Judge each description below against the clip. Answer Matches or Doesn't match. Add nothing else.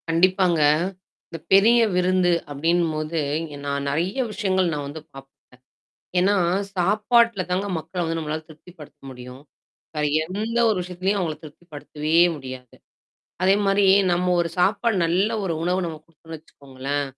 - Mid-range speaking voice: Matches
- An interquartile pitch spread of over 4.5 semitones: Doesn't match